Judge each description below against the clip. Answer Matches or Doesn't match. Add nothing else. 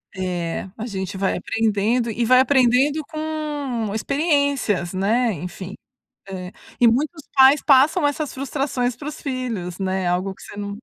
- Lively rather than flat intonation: Matches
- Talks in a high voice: Matches